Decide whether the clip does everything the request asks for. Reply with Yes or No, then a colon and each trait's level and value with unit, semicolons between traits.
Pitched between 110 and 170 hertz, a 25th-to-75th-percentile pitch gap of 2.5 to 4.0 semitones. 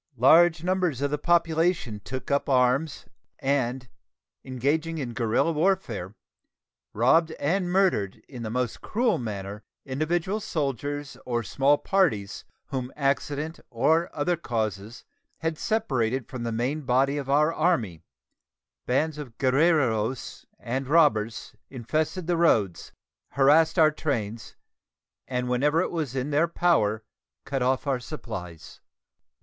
No: medium, 140 Hz; average, 5.2 semitones